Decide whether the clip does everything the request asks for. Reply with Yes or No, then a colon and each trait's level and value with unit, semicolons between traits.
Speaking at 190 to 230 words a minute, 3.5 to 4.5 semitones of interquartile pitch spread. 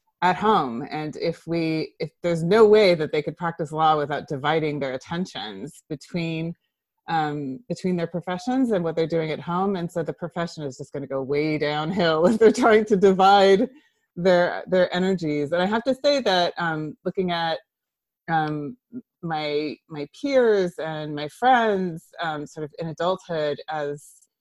No: average, 170 wpm; average, 3.8 semitones